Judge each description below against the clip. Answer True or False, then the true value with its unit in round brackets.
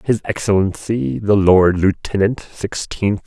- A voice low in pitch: True (95 Hz)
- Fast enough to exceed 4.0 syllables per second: False (3.9 syllables/s)